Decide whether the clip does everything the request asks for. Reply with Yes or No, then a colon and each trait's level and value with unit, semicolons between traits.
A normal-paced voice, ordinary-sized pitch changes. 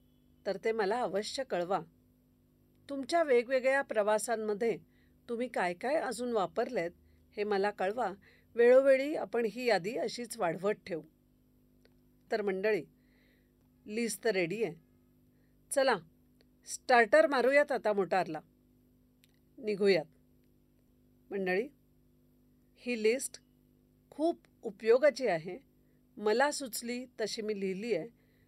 Yes: average, 100 wpm; average, 4.6 semitones